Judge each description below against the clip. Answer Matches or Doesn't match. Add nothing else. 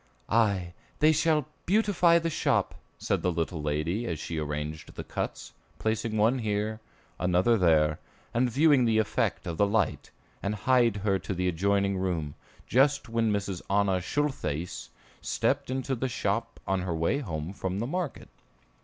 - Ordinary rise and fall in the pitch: Doesn't match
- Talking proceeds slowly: Doesn't match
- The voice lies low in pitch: Matches